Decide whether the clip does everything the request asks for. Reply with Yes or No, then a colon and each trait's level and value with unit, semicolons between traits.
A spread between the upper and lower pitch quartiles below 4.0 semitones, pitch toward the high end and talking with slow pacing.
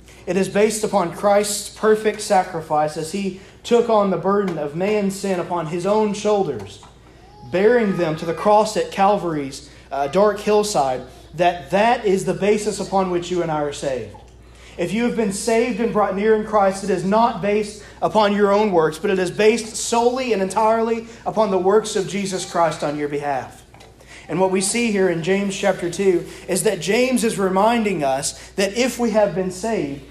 No: average, 3.5 semitones; high, 195 Hz; average, 195 wpm